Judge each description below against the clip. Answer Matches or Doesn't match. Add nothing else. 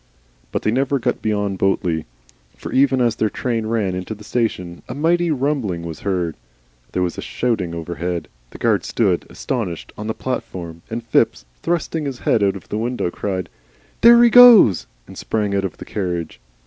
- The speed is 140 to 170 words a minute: Doesn't match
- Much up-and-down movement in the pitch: Matches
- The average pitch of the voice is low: Matches